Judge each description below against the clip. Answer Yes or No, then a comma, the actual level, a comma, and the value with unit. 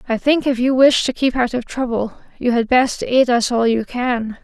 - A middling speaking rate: No, fast, 245 wpm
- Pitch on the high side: Yes, high, 245 Hz